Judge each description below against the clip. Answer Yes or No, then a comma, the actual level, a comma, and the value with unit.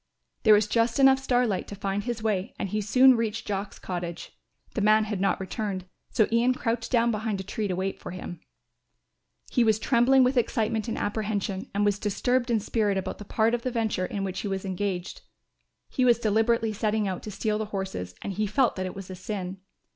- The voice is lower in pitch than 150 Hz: No, high, 210 Hz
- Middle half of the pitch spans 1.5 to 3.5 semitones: Yes, average, 3.0 semitones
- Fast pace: Yes, fast, 215 wpm